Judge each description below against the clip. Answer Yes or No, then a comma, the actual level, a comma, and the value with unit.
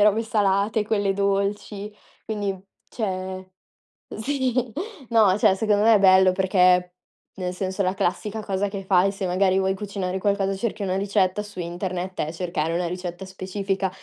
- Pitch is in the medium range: No, high, 195 Hz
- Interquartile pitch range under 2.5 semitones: Yes, narrow, 1.8 semitones